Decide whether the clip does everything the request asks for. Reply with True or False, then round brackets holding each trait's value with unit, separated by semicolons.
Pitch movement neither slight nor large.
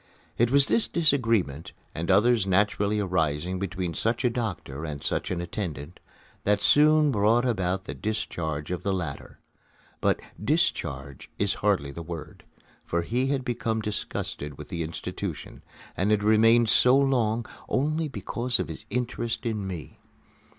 False (5.8 semitones)